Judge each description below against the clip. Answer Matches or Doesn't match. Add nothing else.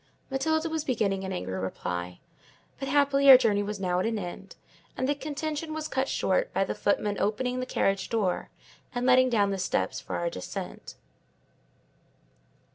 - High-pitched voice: Matches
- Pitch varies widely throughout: Matches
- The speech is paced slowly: Doesn't match